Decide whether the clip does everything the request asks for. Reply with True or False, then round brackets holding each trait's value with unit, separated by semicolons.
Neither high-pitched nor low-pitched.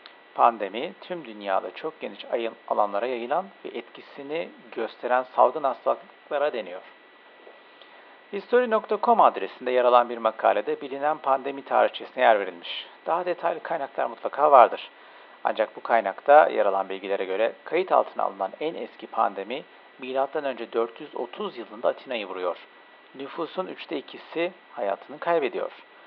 True (150 Hz)